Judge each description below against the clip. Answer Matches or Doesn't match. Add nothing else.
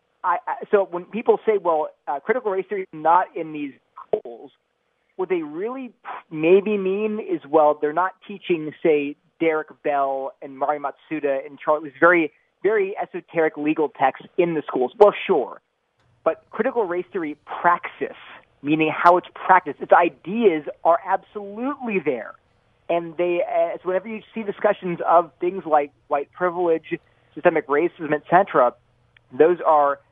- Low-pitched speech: Doesn't match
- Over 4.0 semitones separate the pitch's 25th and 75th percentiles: Matches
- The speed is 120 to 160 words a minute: Matches